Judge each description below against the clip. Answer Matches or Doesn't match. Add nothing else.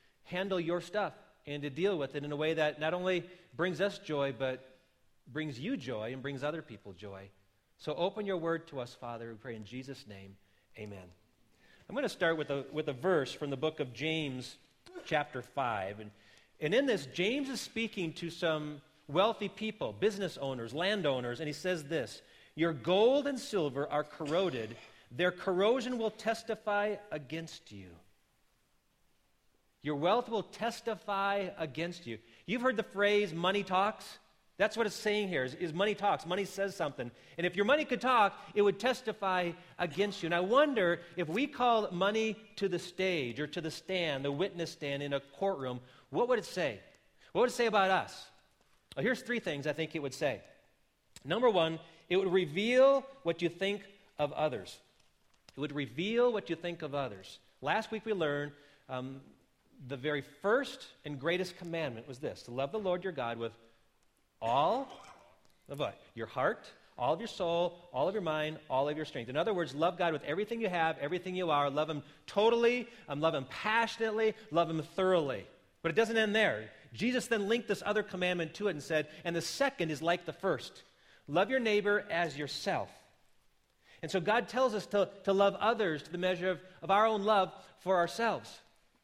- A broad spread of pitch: Matches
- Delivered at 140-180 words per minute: Doesn't match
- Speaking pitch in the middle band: Matches